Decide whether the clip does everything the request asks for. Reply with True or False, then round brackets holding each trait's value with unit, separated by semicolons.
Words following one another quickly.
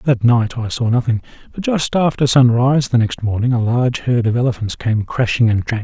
True (225 wpm)